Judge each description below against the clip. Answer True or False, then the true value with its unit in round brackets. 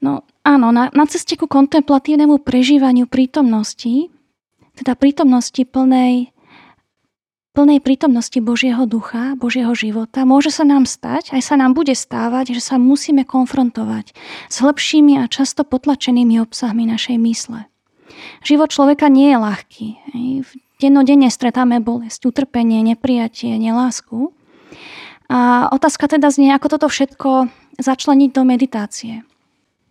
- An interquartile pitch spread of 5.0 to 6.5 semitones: False (2.8 semitones)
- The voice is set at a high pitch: True (260 Hz)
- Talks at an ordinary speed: True (120 wpm)